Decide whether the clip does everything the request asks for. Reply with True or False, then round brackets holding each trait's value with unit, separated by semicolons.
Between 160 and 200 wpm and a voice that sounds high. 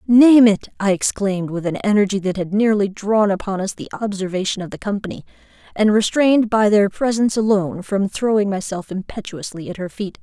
True (180 wpm; 200 Hz)